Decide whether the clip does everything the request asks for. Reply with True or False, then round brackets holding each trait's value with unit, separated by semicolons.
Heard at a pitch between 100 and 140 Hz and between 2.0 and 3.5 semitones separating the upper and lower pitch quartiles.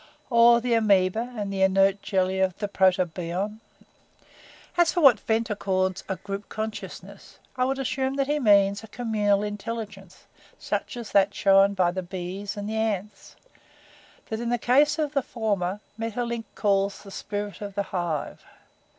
False (205 Hz; 3.2 semitones)